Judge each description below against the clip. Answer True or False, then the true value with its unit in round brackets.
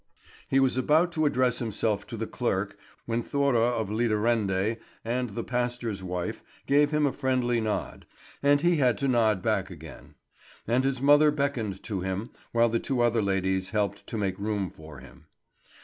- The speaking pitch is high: False (115 Hz)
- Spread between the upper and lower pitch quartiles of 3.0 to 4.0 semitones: False (4.5 semitones)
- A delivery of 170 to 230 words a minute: True (175 wpm)